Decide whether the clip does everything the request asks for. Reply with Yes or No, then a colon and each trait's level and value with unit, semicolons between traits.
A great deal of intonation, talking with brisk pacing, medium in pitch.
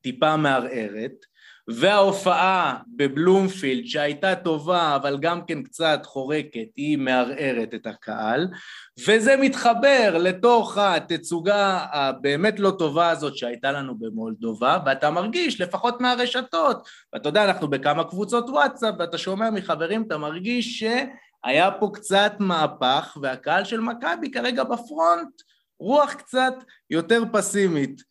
No: wide, 7.3 semitones; average, 115 wpm; medium, 175 Hz